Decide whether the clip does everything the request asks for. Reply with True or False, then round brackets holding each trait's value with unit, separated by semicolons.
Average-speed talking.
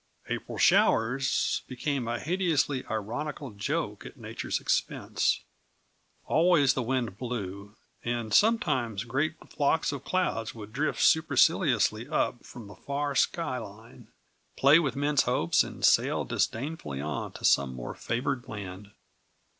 False (130 wpm)